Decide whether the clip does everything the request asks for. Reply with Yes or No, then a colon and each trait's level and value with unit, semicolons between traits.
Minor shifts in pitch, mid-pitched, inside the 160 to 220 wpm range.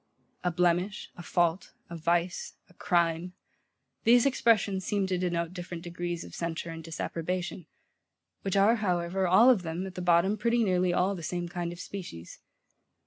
Yes: narrow, 2.0 semitones; medium, 180 Hz; average, 165 wpm